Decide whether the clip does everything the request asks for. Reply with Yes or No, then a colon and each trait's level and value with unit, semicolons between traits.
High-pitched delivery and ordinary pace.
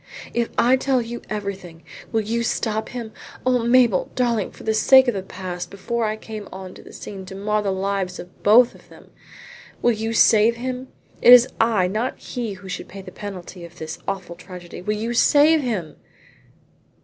Yes: high, 215 Hz; average, 190 wpm